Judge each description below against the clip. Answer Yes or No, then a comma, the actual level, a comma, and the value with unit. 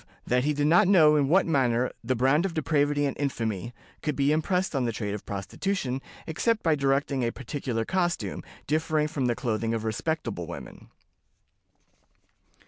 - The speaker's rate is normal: Yes, average, 165 wpm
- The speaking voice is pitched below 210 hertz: Yes, medium, 140 Hz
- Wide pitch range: No, average, 4.8 semitones